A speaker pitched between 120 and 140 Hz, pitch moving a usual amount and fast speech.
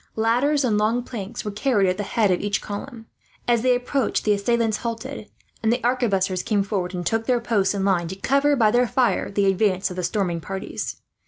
No: high, 215 Hz; average, 3.7 semitones; fast, 215 wpm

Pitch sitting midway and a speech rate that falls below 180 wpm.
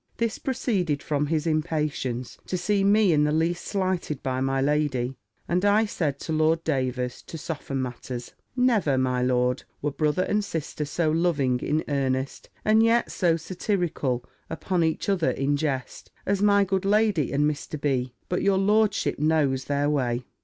Yes: medium, 155 Hz; average, 165 wpm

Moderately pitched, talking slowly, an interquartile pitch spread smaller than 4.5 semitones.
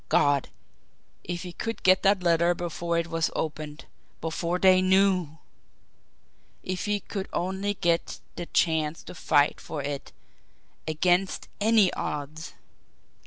Yes: medium, 175 Hz; slow, 130 wpm; average, 2.9 semitones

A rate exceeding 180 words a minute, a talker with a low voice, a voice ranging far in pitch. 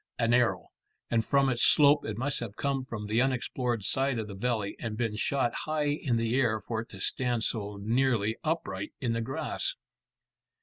No: average, 190 wpm; low, 120 Hz; average, 3.4 semitones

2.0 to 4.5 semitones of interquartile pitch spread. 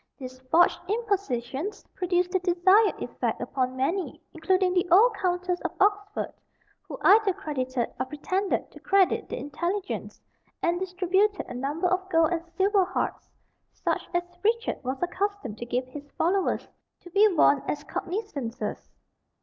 No: wide, 5.4 semitones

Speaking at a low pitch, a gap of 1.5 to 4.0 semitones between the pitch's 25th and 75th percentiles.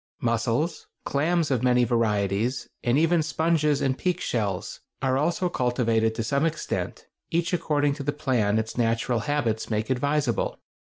No: low, 130 Hz; average, 4.9 semitones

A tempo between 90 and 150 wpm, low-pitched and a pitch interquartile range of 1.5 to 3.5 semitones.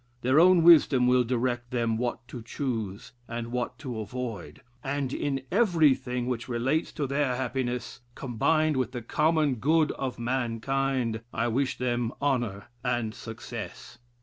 Yes: average, 145 wpm; low, 125 Hz; average, 2.7 semitones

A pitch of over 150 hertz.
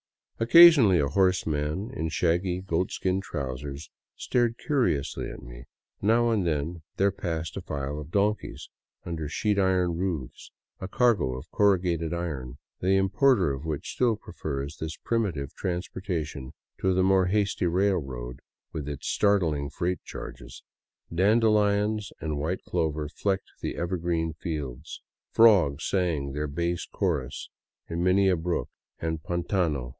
No: very low, 85 Hz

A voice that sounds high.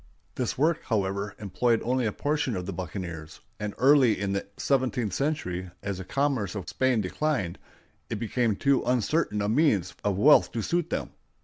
No: low, 110 Hz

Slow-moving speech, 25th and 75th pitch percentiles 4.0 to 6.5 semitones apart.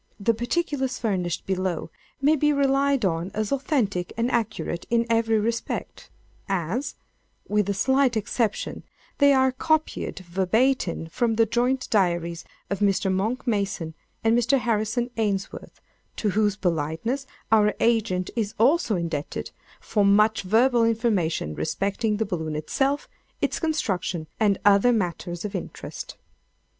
Yes: slow, 130 wpm; average, 4.7 semitones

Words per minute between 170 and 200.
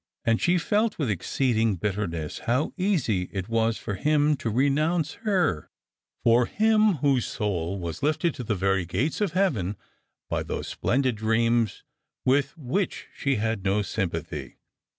No: average, 150 wpm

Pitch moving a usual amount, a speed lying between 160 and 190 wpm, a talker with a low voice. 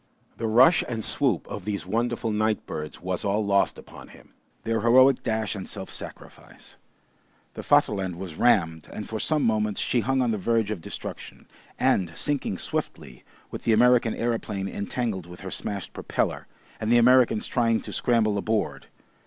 Yes: average, 3.3 semitones; average, 170 wpm; low, 110 Hz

